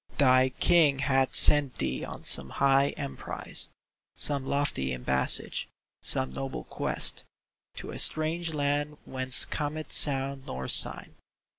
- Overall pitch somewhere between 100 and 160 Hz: Yes, low, 135 Hz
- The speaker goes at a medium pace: No, slow, 125 wpm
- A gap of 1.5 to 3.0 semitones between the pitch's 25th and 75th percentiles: Yes, narrow, 2.4 semitones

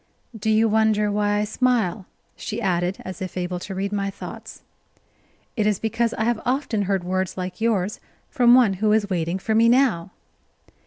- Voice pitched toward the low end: No, high, 210 Hz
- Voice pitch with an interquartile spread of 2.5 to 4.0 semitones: Yes, average, 3.0 semitones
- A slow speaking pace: No, average, 180 wpm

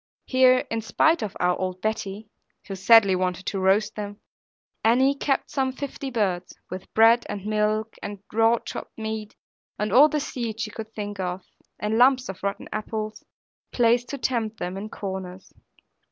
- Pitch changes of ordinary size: Yes, average, 3.3 semitones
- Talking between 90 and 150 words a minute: No, average, 170 wpm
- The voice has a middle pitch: No, high, 215 Hz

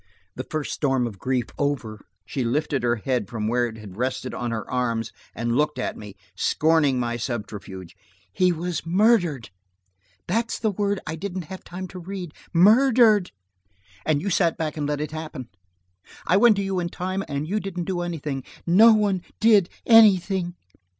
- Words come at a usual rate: Yes, average, 175 wpm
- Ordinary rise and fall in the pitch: No, wide, 7.3 semitones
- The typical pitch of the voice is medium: Yes, medium, 155 Hz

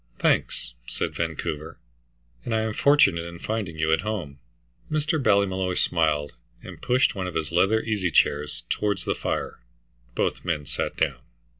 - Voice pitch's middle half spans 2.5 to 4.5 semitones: No, average, 5.3 semitones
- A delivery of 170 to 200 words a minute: No, average, 155 wpm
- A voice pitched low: Yes, very low, 90 Hz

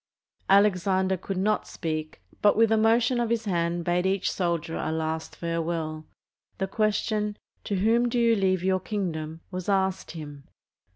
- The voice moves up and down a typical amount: Yes, average, 4.0 semitones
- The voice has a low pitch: No, high, 190 Hz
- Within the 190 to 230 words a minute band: No, average, 160 wpm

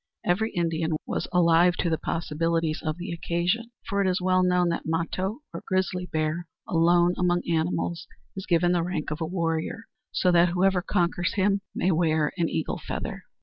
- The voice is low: No, medium, 175 Hz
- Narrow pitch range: Yes, narrow, 1.7 semitones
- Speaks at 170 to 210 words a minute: Yes, average, 180 wpm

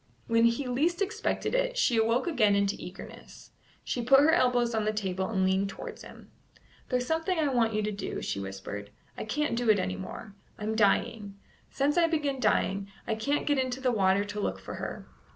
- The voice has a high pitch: Yes, high, 230 Hz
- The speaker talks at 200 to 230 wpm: Yes, fast, 205 wpm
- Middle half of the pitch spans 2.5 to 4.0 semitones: No, wide, 5.5 semitones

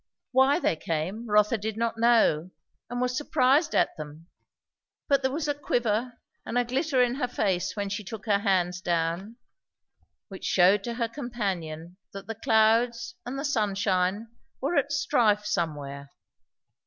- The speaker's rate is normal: Yes, average, 155 wpm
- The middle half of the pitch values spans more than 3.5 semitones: Yes, average, 4.9 semitones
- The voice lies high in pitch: Yes, high, 220 Hz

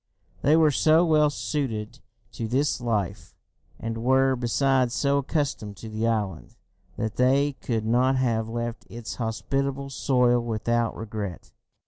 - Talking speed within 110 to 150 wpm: Yes, slow, 135 wpm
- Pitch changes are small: No, average, 3.5 semitones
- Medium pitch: No, low, 120 Hz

